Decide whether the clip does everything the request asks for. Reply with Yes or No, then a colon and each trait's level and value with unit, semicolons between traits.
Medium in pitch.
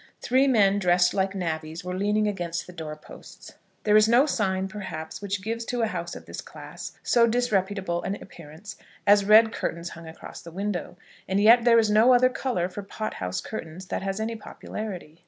No: high, 200 Hz